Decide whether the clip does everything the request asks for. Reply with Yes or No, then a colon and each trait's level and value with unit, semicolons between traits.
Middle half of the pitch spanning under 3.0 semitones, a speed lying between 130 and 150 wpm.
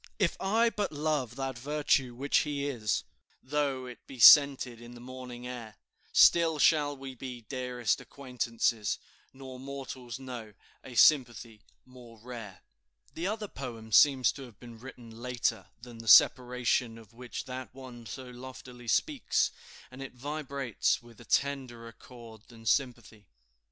Yes: narrow, 2.6 semitones; average, 145 wpm